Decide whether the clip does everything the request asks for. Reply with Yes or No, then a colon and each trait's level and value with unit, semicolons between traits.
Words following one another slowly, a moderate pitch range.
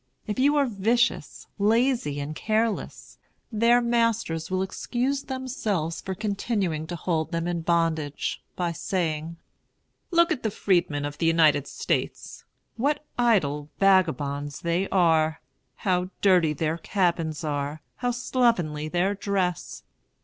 No: slow, 130 wpm; wide, 6.3 semitones